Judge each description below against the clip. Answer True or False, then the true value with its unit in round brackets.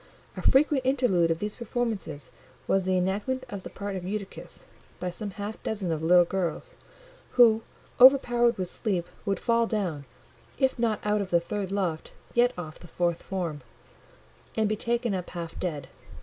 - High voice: True (200 Hz)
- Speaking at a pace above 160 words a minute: True (170 wpm)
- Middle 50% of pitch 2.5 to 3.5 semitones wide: False (4.8 semitones)